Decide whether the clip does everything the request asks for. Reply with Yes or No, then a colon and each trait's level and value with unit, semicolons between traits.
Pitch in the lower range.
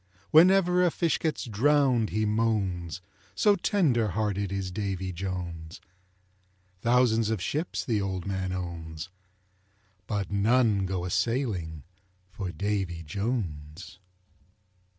Yes: low, 100 Hz